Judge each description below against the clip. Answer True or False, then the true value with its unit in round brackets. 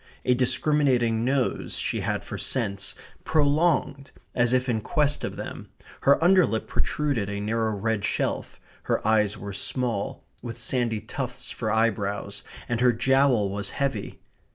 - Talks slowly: False (145 wpm)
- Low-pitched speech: True (120 Hz)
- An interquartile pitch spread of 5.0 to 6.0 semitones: False (3.9 semitones)